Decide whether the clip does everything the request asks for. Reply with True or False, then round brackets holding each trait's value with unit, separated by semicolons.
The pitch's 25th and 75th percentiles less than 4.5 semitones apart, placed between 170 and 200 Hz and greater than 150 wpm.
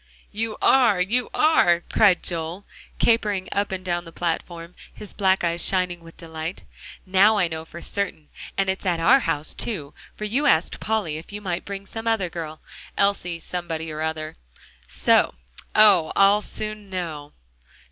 True (3.7 semitones; 185 Hz; 165 wpm)